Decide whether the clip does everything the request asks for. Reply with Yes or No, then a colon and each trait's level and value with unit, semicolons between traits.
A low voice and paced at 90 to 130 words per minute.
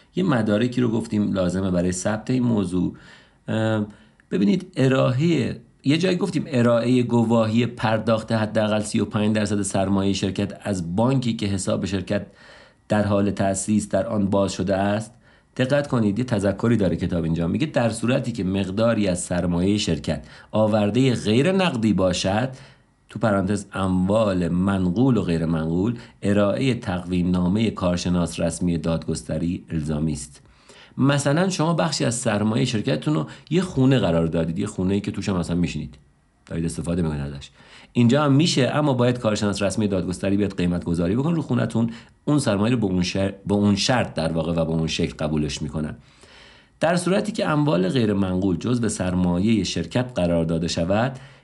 No: low, 105 Hz; fast, 155 wpm